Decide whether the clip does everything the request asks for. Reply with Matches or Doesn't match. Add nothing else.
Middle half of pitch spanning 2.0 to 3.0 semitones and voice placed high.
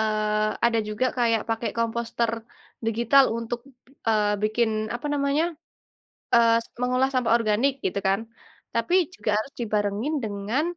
Matches